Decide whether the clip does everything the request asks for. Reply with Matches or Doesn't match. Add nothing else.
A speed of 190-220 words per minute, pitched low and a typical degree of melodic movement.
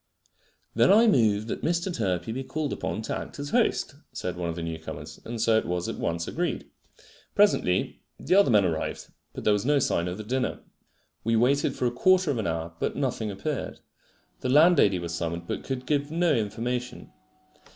Doesn't match